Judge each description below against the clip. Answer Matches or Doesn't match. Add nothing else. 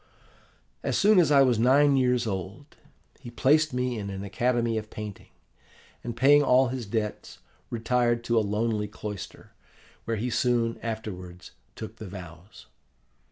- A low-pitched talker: Matches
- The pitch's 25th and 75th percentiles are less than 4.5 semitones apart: Matches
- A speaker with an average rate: Matches